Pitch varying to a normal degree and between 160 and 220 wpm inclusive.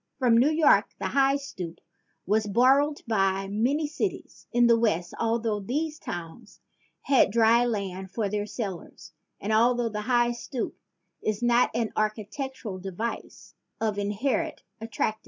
No: average, 3.6 semitones; average, 140 wpm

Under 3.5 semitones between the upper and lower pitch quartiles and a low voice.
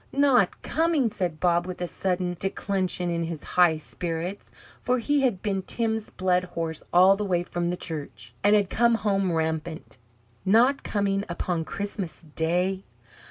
No: average, 3.1 semitones; medium, 185 Hz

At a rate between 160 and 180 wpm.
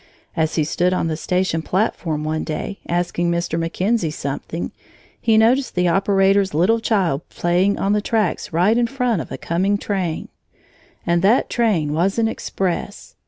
Yes: average, 165 wpm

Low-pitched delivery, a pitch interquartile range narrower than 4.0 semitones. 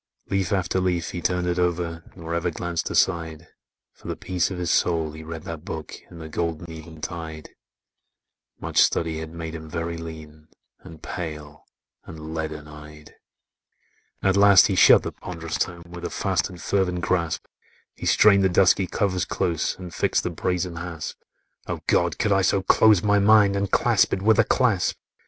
Yes: very low, 85 Hz; narrow, 2.5 semitones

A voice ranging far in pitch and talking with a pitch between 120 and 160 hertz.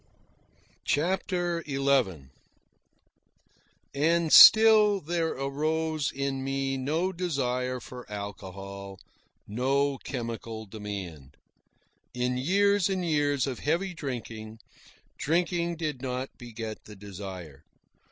Yes: wide, 6.9 semitones; low, 135 Hz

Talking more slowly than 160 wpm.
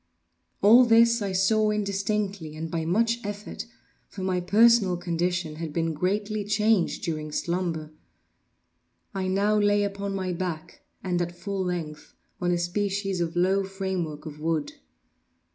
Yes: average, 140 wpm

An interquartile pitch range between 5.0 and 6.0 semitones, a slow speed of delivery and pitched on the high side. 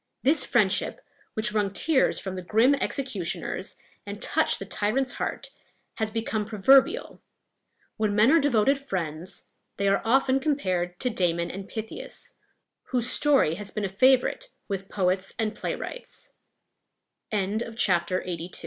Yes: average, 5.3 semitones; slow, 130 wpm; high, 215 Hz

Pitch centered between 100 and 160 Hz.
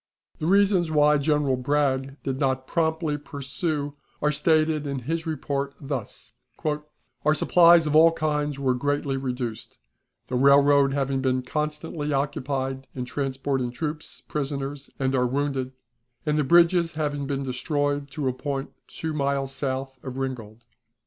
Yes: medium, 140 Hz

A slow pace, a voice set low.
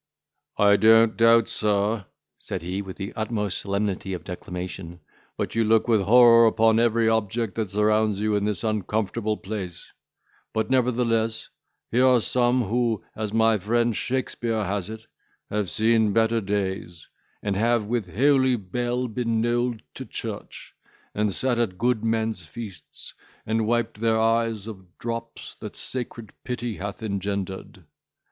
No: average, 145 wpm; low, 110 Hz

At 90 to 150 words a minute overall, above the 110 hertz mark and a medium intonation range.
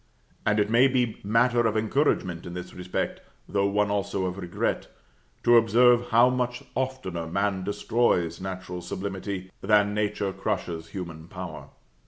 No: average, 145 wpm; low, 100 Hz; average, 4.2 semitones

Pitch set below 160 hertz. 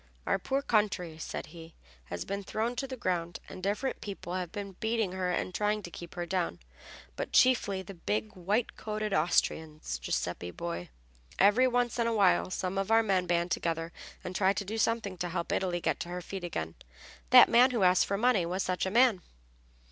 No: high, 190 Hz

